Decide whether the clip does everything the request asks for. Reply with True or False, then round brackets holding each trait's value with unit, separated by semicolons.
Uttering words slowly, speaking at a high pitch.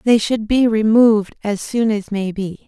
False (200 wpm; 215 Hz)